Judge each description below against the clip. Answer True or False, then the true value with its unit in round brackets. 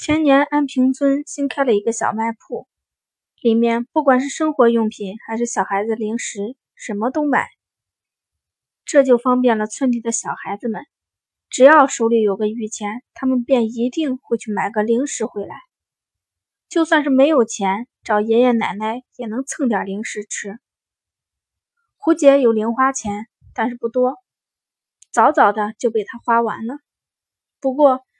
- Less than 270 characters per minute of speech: True (225 characters per minute)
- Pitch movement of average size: True (3.8 semitones)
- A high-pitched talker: True (235 Hz)